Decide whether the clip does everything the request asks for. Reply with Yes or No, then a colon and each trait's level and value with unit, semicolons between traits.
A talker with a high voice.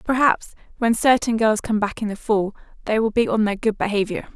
Yes: high, 220 Hz